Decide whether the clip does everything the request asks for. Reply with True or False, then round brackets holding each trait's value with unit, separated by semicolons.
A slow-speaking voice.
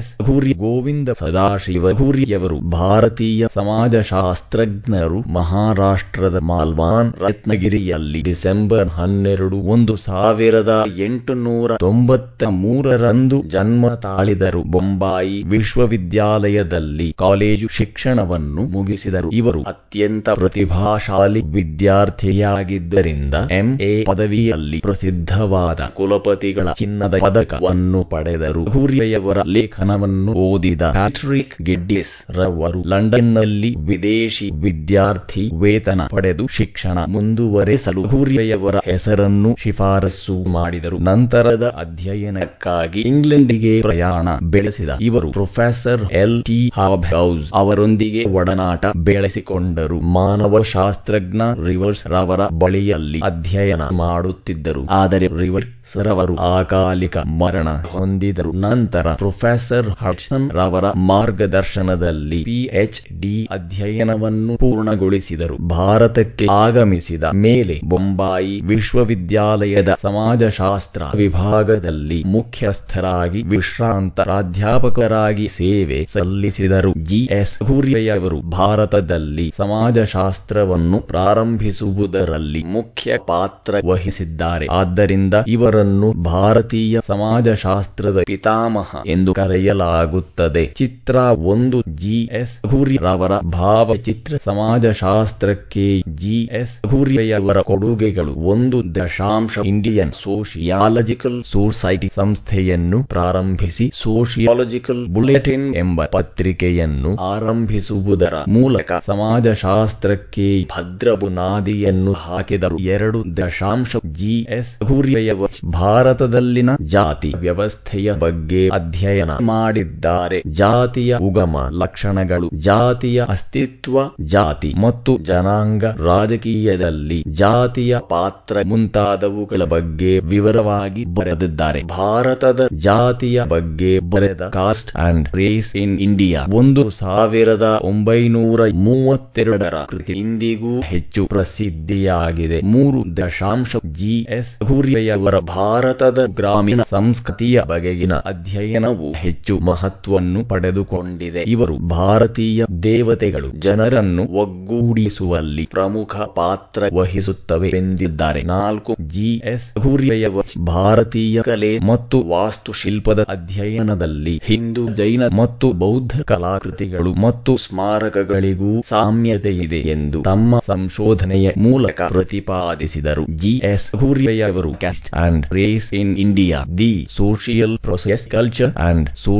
True (80 wpm)